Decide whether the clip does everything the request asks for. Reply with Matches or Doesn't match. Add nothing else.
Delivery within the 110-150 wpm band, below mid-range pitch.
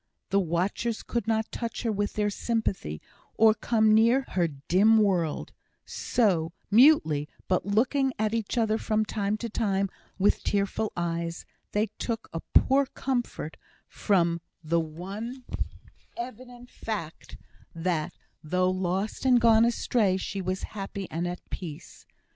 Doesn't match